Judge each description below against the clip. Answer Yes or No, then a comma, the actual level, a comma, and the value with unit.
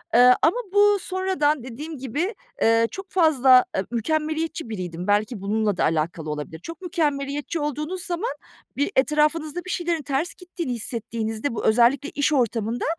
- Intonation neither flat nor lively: No, wide, 6.3 semitones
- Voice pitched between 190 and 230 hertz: No, very high, 285 Hz